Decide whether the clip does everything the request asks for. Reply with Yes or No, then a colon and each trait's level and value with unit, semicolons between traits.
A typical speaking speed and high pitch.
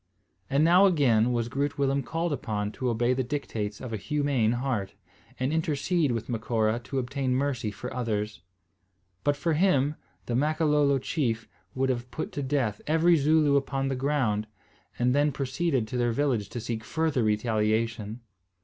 No: average, 165 wpm; low, 130 Hz